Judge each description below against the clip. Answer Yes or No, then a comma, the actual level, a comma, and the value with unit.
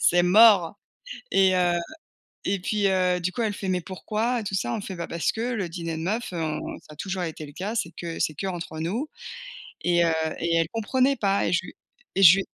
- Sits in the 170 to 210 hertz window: Yes, medium, 185 Hz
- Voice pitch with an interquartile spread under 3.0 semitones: No, average, 3.3 semitones